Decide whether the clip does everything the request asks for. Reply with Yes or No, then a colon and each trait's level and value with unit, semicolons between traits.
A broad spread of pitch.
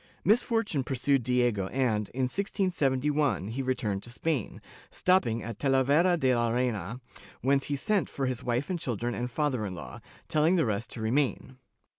No: average, 4.1 semitones